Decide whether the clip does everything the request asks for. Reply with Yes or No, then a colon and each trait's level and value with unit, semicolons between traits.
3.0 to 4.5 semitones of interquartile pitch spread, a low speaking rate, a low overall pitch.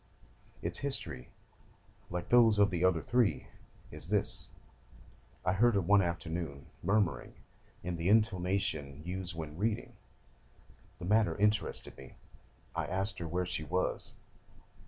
Yes: average, 3.7 semitones; slow, 130 wpm; very low, 90 Hz